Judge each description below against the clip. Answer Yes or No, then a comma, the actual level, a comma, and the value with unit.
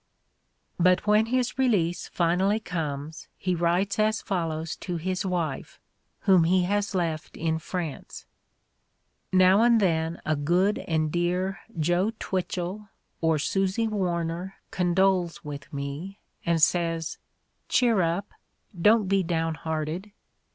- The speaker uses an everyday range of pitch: Yes, average, 3.0 semitones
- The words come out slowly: Yes, slow, 125 wpm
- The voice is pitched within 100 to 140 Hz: No, medium, 180 Hz